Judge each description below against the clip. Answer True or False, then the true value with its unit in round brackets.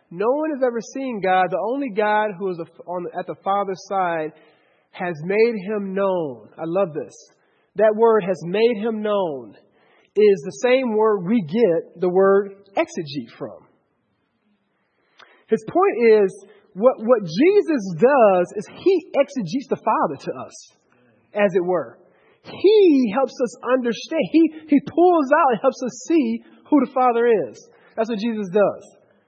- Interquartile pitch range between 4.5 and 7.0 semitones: True (5.2 semitones)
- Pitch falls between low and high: False (220 Hz)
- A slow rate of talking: False (160 wpm)